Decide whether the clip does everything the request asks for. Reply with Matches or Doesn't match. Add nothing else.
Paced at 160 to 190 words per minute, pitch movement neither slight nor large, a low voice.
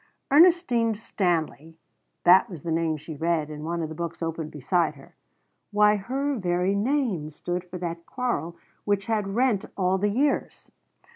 Doesn't match